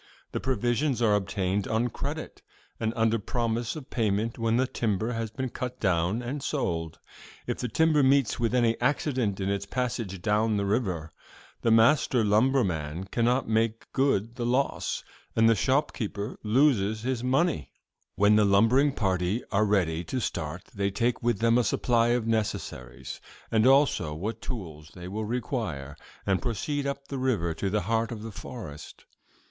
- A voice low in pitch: Yes, low, 115 Hz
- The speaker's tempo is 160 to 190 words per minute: Yes, average, 165 wpm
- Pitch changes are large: No, average, 4.0 semitones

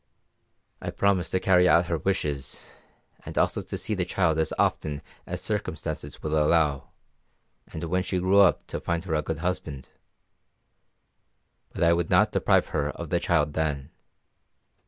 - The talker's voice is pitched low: Yes, very low, 85 Hz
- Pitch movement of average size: Yes, average, 3.1 semitones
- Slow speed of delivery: No, average, 160 wpm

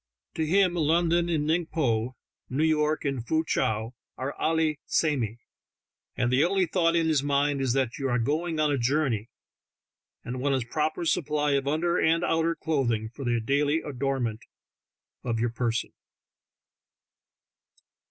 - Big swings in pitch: No, average, 4.3 semitones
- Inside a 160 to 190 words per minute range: No, average, 150 wpm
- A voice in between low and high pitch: Yes, medium, 145 Hz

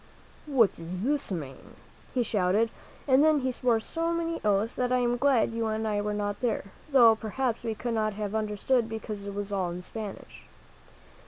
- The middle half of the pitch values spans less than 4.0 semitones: Yes, average, 3.5 semitones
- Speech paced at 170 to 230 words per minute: Yes, average, 190 wpm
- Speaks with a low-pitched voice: No, high, 220 Hz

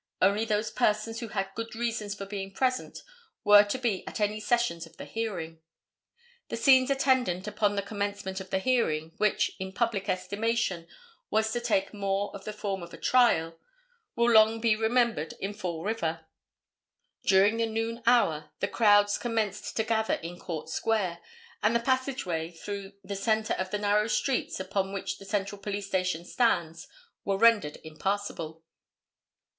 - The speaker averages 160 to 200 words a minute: Yes, average, 165 wpm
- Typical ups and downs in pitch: Yes, average, 3.0 semitones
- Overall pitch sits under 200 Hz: No, high, 205 Hz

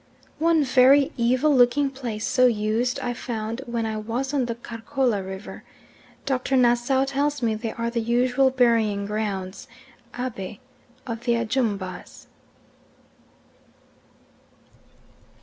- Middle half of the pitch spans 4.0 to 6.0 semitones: No, average, 3.1 semitones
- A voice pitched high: Yes, high, 240 Hz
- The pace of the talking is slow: Yes, slow, 115 wpm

